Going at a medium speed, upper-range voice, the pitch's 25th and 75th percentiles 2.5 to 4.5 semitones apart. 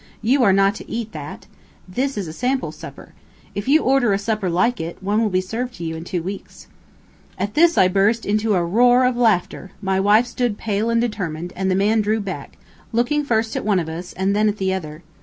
No: fast, 230 wpm; high, 205 Hz; average, 3.9 semitones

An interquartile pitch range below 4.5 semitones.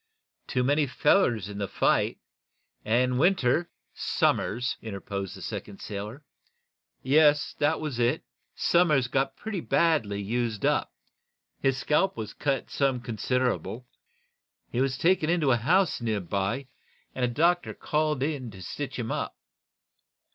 No: average, 4.9 semitones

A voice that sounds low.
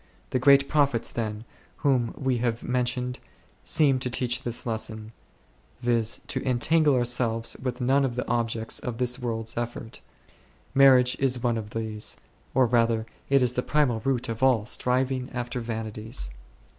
Yes: low, 125 Hz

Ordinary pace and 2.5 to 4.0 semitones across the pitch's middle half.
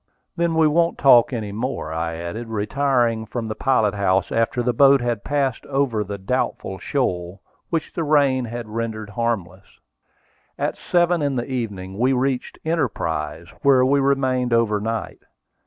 No: average, 155 wpm; average, 4.6 semitones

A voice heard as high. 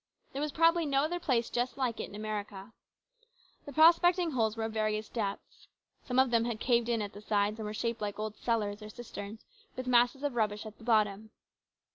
Yes: high, 225 Hz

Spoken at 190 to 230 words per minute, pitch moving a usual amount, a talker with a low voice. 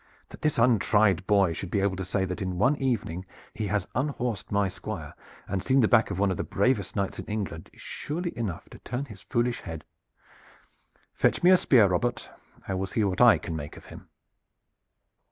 Yes: fast, 205 wpm; average, 4.3 semitones; low, 100 Hz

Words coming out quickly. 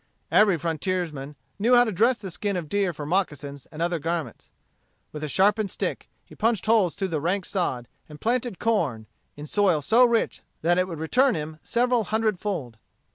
No: average, 185 wpm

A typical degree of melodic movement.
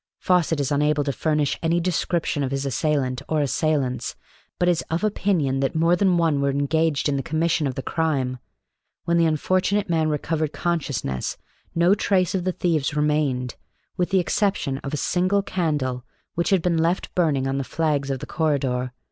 Yes: average, 3.8 semitones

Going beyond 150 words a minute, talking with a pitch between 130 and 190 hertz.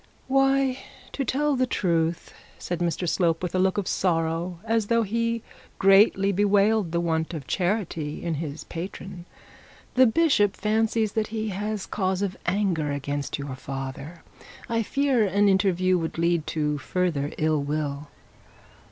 No: average, 145 wpm; medium, 185 Hz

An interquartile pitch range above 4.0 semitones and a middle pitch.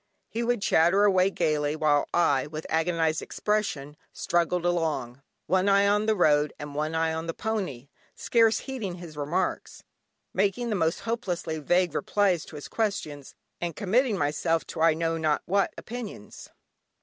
Yes: average, 4.6 semitones; medium, 170 Hz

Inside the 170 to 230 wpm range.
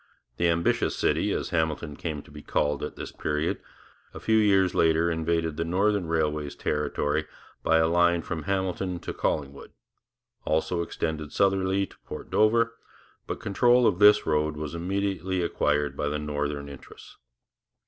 No: average, 155 wpm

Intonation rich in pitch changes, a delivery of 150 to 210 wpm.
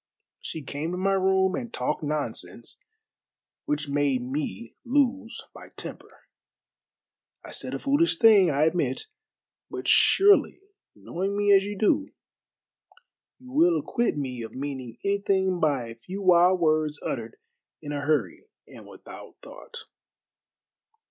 No: wide, 6.4 semitones; slow, 135 wpm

